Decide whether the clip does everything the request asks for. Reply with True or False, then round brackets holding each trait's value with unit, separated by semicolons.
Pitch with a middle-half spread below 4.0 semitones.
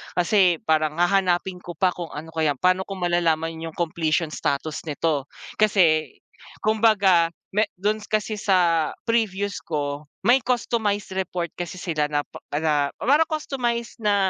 False (4.4 semitones)